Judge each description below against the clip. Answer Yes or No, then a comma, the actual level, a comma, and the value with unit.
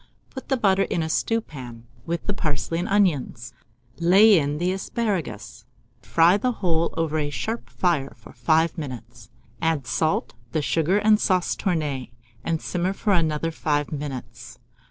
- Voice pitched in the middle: Yes, medium, 165 Hz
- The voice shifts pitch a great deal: No, average, 4.8 semitones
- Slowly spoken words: No, average, 155 wpm